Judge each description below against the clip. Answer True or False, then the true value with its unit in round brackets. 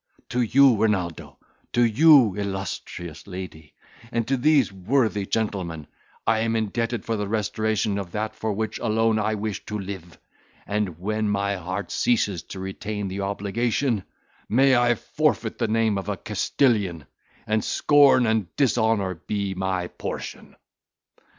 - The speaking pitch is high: False (105 Hz)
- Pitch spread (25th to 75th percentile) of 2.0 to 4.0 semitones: True (3.0 semitones)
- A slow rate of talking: False (145 wpm)